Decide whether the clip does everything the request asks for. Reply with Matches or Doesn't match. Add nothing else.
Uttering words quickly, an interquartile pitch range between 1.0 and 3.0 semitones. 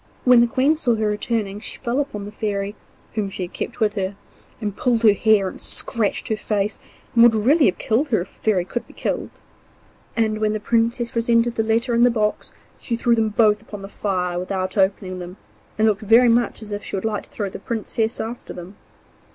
Matches